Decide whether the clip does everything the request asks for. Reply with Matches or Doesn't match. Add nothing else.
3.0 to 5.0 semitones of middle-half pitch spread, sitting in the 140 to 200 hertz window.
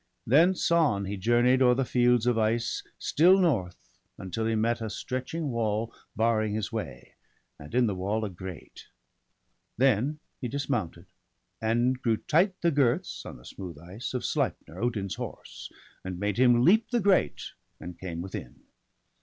Doesn't match